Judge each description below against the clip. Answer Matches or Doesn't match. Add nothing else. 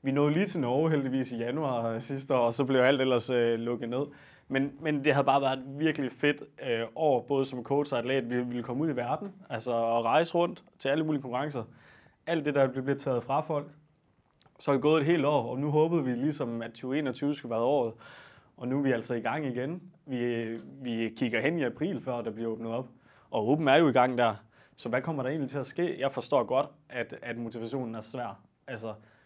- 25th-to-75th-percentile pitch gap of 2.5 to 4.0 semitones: Matches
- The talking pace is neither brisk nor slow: Doesn't match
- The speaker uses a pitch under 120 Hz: Doesn't match